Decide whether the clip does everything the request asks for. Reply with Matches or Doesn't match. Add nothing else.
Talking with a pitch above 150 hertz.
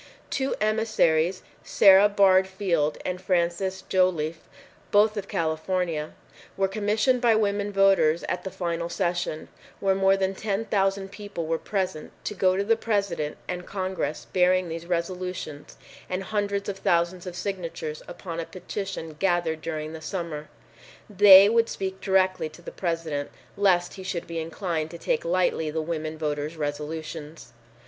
Matches